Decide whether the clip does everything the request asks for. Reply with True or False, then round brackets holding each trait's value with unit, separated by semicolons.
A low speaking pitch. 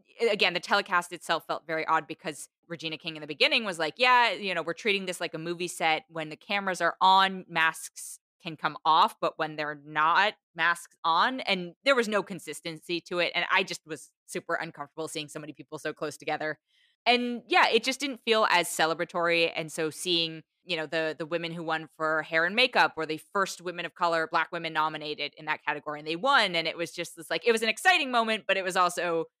False (170 Hz)